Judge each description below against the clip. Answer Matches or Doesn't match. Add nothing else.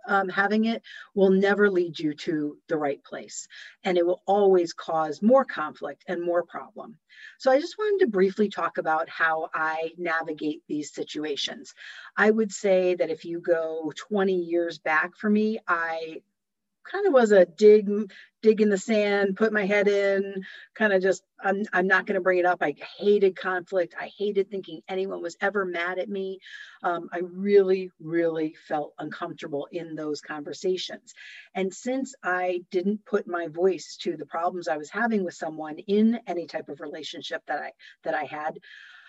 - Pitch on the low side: Doesn't match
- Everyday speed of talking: Matches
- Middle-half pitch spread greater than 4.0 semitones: Doesn't match